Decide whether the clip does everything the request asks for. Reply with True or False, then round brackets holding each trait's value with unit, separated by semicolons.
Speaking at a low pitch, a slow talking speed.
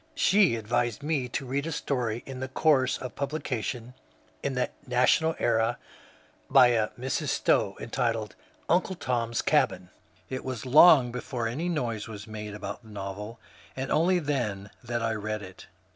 False (125 Hz; 165 wpm)